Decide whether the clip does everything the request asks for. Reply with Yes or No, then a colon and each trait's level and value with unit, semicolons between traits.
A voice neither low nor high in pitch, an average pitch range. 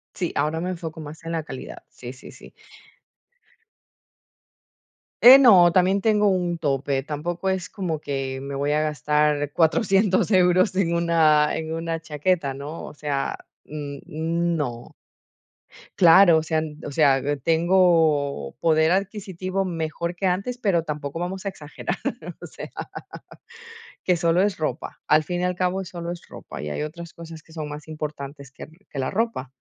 Yes: medium, 165 Hz; average, 3.4 semitones